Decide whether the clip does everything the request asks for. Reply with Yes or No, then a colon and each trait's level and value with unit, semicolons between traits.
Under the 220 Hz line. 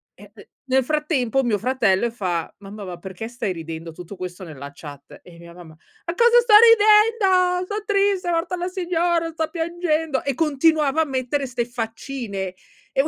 No: very high, 270 Hz